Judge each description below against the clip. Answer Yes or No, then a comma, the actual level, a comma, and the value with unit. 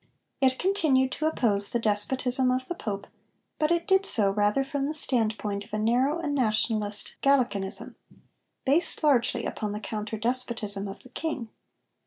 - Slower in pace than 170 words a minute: Yes, average, 160 wpm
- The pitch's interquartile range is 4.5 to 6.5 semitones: Yes, average, 4.8 semitones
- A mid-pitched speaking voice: No, high, 245 Hz